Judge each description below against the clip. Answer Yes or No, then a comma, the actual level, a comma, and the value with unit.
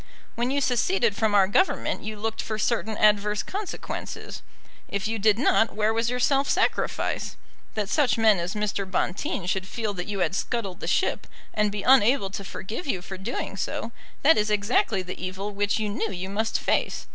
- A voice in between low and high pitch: No, high, 210 Hz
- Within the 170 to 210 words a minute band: Yes, average, 190 wpm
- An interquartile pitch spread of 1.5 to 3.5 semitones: Yes, average, 2.8 semitones